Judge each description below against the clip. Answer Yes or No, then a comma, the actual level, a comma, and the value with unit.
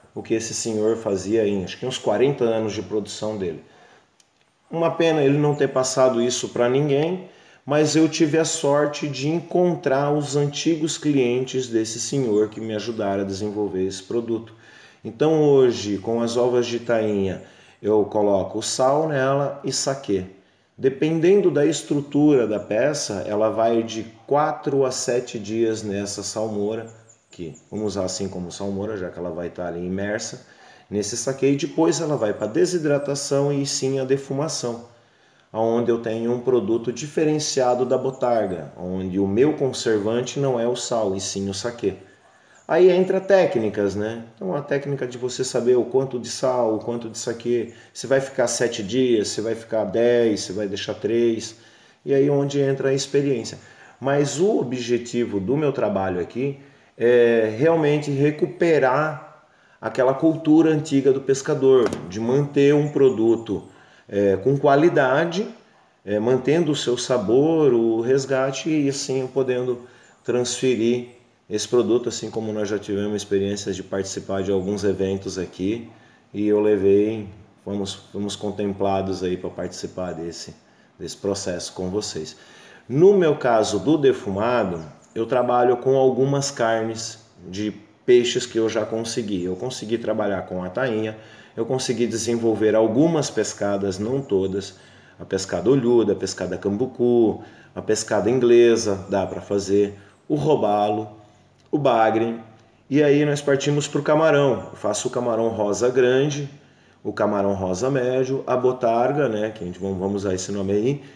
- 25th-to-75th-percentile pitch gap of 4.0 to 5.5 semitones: Yes, average, 4.7 semitones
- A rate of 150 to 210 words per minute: Yes, average, 155 wpm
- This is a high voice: No, low, 120 Hz